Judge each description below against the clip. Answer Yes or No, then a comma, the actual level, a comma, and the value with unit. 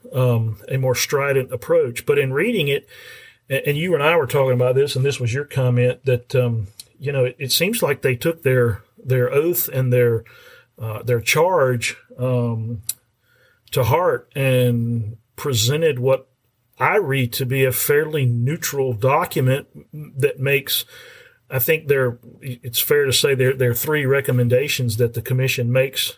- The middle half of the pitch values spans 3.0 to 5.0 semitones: No, narrow, 2.6 semitones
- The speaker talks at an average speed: Yes, average, 165 wpm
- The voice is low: Yes, low, 130 Hz